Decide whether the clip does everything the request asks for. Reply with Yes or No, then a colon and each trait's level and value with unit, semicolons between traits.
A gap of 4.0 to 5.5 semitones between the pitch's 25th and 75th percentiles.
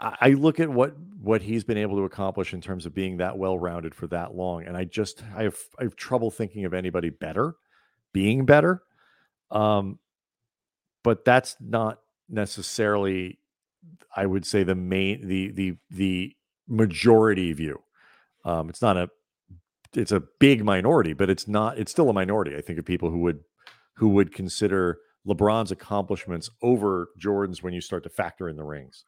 No: average, 3.6 semitones